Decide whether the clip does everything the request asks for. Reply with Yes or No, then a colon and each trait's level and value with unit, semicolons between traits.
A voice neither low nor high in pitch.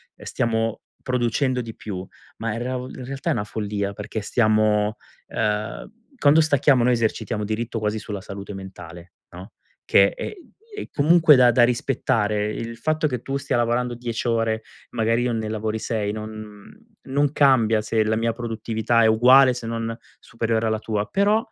No: low, 115 Hz